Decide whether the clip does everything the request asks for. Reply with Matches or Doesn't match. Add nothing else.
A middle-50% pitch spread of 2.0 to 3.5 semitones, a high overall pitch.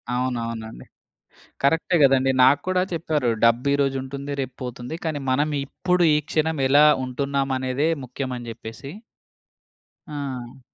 Doesn't match